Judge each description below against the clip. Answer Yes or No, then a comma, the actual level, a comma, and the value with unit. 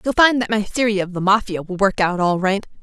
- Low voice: No, high, 200 Hz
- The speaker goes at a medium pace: No, fast, 275 wpm